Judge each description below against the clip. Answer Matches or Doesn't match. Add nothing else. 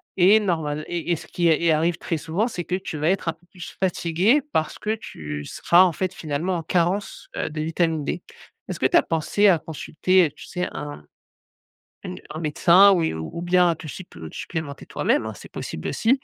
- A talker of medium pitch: Matches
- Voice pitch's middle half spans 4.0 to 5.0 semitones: Doesn't match